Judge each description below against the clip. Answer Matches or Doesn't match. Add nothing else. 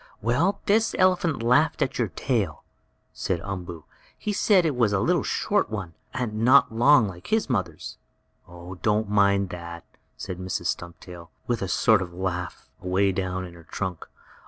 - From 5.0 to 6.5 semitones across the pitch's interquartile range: Matches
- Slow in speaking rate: Doesn't match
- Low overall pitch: Matches